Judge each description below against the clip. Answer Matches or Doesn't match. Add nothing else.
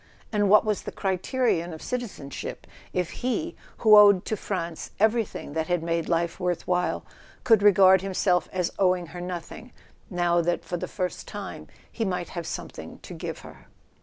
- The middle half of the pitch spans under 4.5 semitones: Matches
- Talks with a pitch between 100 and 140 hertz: Doesn't match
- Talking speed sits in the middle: Matches